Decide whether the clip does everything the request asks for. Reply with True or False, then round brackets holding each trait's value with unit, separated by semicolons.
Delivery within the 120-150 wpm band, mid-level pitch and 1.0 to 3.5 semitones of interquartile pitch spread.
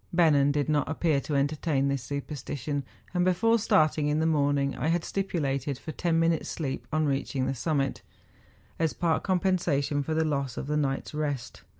False (180 wpm; 150 Hz; 2.8 semitones)